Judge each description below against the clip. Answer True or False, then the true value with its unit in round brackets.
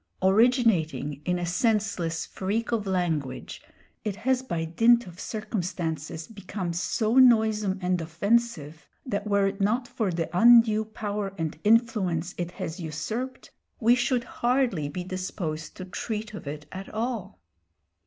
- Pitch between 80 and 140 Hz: False (200 Hz)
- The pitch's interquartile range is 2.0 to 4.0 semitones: False (4.9 semitones)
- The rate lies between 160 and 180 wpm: False (140 wpm)